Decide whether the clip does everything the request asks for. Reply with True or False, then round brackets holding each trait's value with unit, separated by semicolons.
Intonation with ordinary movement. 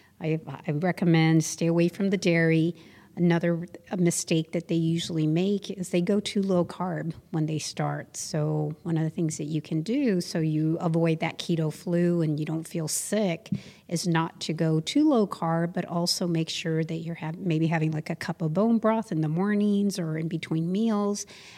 False (2.1 semitones)